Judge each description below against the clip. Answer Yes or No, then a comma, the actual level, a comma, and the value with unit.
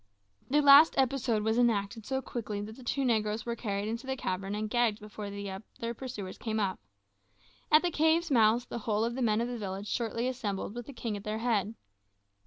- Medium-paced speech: No, fast, 210 wpm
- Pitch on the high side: Yes, high, 225 Hz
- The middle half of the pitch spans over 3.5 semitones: No, average, 2.9 semitones